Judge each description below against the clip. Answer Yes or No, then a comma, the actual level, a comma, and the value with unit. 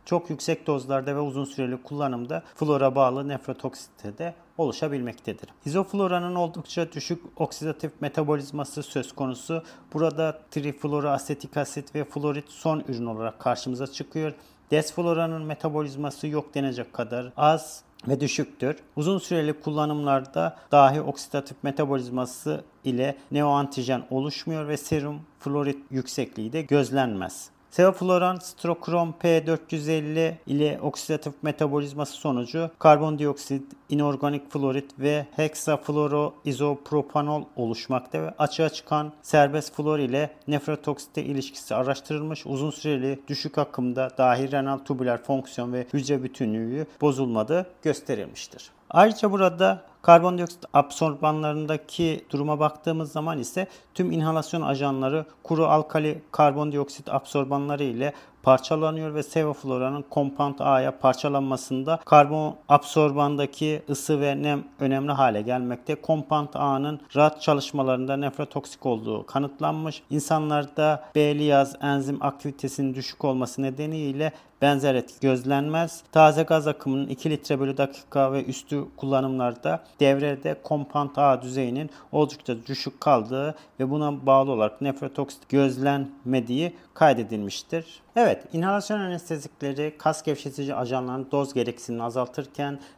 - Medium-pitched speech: Yes, medium, 145 Hz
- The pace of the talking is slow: No, average, 110 wpm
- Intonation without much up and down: Yes, narrow, 2.2 semitones